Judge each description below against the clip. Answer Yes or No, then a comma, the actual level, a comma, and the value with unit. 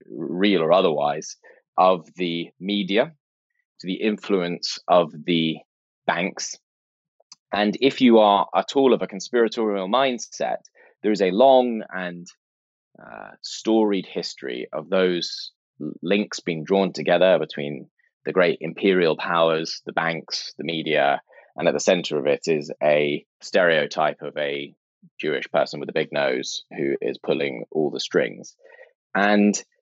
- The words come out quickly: No, average, 140 wpm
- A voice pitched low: Yes, very low, 95 Hz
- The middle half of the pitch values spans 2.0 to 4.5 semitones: No, average, 4.9 semitones